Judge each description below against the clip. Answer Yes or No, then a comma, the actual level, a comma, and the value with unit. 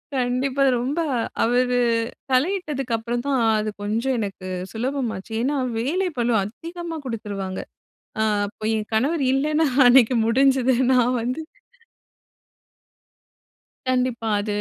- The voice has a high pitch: Yes, very high, 250 Hz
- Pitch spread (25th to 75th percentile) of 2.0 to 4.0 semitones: Yes, average, 3.4 semitones